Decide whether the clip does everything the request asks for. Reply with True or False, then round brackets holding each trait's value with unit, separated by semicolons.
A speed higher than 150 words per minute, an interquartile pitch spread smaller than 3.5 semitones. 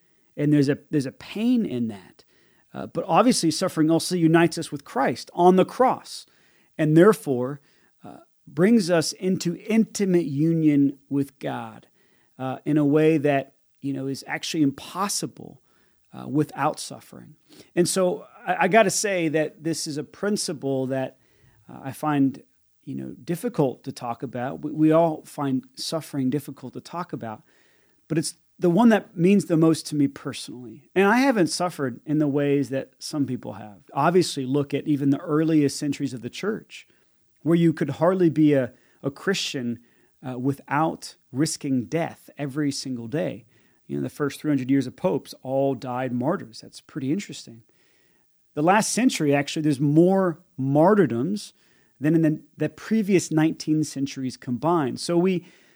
False (165 wpm; 3.9 semitones)